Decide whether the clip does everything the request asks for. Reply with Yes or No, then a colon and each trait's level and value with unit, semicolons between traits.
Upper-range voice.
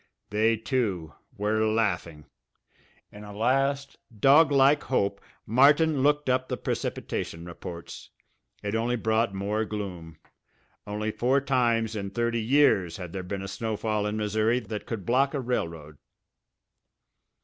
No: low, 110 Hz